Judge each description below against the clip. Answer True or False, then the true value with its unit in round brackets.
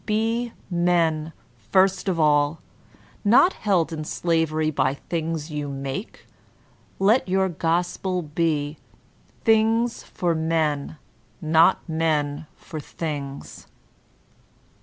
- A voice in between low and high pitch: True (165 Hz)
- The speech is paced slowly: True (100 wpm)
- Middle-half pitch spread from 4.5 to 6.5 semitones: False (3.6 semitones)